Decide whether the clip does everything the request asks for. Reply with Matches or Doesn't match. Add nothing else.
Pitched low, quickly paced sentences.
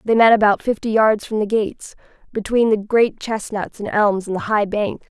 Doesn't match